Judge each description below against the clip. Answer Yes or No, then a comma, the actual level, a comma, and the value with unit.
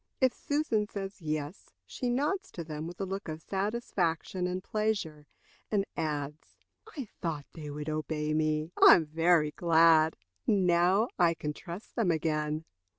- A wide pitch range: No, average, 4.2 semitones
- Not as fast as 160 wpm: Yes, average, 150 wpm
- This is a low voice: No, medium, 170 Hz